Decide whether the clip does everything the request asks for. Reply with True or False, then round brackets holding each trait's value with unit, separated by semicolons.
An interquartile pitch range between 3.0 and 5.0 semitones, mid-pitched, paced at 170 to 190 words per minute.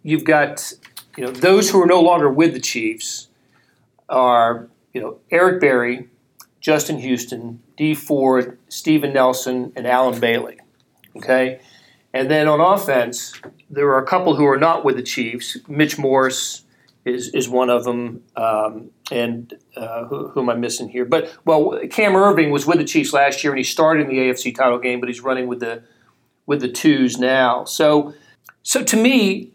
False (3.7 semitones; 130 Hz; 175 wpm)